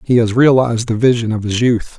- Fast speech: Yes, fast, 240 wpm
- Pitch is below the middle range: Yes, low, 115 Hz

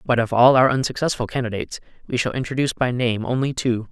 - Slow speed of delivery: No, average, 200 wpm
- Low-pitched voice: Yes, low, 120 Hz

